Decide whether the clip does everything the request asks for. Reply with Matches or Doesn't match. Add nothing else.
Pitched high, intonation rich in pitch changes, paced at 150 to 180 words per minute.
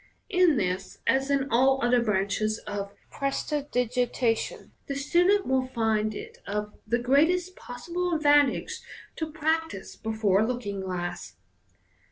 Doesn't match